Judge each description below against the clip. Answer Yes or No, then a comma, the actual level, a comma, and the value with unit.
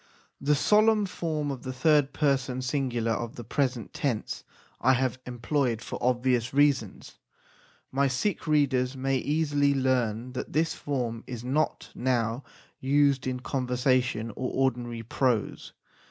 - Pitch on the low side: Yes, low, 130 Hz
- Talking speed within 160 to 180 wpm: No, slow, 135 wpm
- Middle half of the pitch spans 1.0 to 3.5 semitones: Yes, narrow, 2.6 semitones